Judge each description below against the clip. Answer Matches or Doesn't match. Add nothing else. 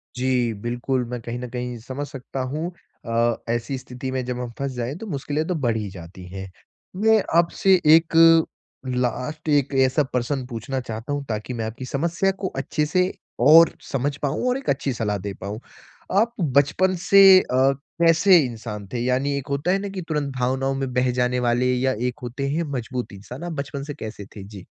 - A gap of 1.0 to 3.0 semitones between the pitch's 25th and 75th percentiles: Doesn't match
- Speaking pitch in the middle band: Doesn't match